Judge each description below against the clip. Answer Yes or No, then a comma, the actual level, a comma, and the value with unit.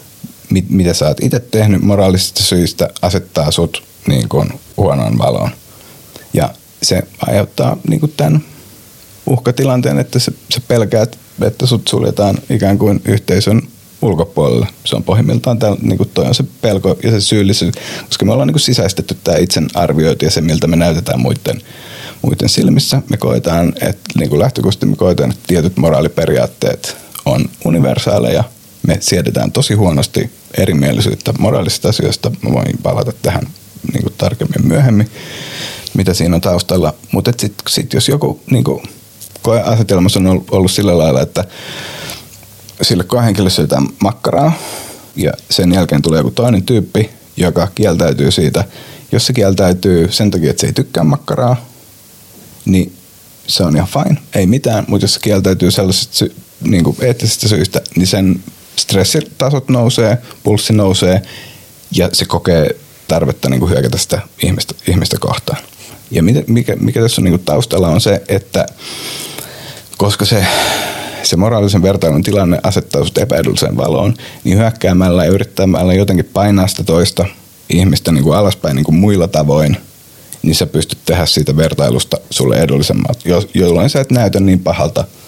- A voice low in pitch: Yes, low, 100 Hz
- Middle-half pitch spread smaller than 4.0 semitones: No, average, 4.8 semitones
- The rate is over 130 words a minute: Yes, average, 145 wpm